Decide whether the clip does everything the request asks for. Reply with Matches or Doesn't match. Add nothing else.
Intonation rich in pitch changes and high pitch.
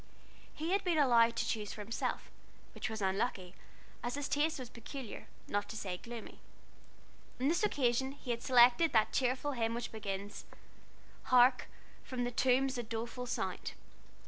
Doesn't match